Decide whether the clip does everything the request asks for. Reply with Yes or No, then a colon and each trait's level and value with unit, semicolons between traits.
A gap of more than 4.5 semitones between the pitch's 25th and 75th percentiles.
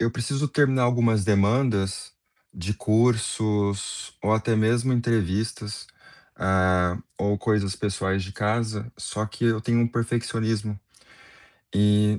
No: narrow, 2.6 semitones